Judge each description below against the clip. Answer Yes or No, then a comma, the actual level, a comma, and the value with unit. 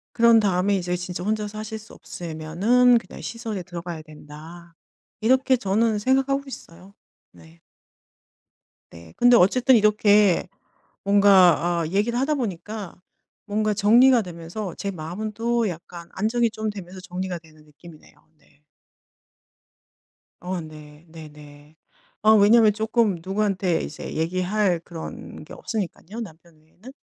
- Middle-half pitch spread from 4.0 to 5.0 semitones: Yes, average, 4.4 semitones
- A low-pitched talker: No, high, 195 Hz